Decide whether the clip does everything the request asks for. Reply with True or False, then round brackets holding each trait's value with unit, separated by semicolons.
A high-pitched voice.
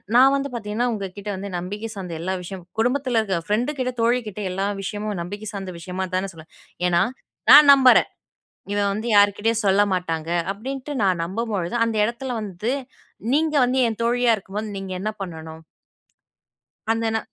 True (210 Hz)